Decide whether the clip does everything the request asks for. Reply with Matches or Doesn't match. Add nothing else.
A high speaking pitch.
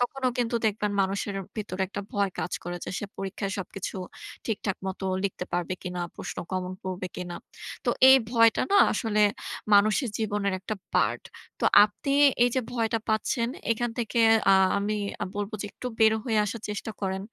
Matches